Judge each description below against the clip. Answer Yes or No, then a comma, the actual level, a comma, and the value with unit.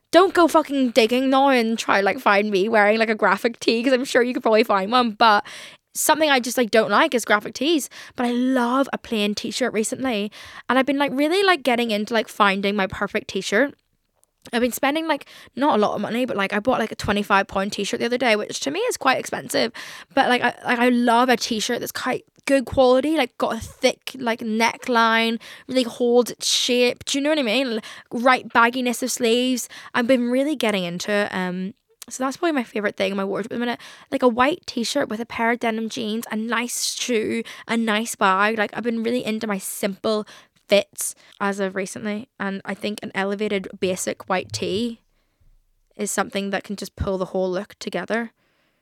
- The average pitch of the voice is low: No, high, 230 Hz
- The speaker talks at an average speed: No, fast, 225 wpm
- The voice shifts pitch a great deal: No, average, 3.6 semitones